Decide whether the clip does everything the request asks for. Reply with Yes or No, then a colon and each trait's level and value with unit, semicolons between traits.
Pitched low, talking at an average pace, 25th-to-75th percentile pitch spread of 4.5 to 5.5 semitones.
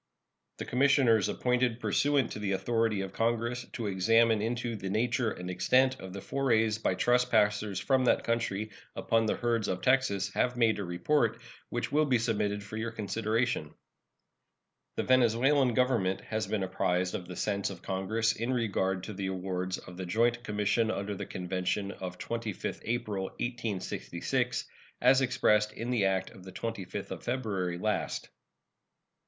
No: low, 110 Hz; average, 160 wpm; average, 3.9 semitones